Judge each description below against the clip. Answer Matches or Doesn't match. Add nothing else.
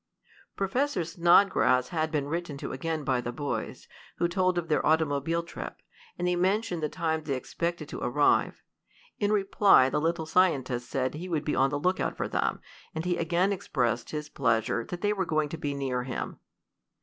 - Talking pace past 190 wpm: Doesn't match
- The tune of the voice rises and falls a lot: Doesn't match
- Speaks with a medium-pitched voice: Matches